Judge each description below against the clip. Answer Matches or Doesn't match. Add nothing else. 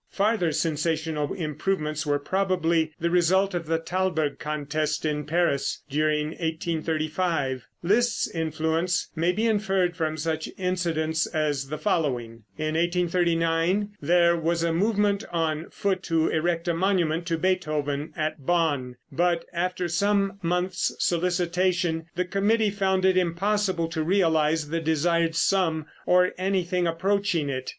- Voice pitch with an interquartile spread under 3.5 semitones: Matches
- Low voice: Doesn't match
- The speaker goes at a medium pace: Doesn't match